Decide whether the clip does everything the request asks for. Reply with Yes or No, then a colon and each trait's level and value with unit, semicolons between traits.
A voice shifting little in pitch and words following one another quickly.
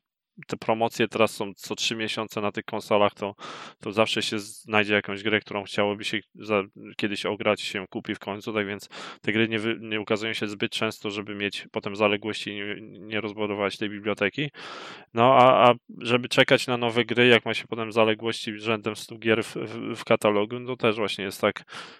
Yes: narrow, 1.6 semitones; fast, 200 wpm